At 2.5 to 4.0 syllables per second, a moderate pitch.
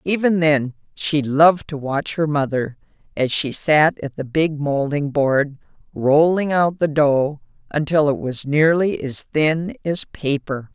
Yes: 3.9 syllables/s; medium, 150 Hz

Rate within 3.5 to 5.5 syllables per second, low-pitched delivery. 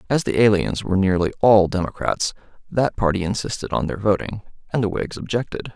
No: 6.0 syllables/s; low, 100 Hz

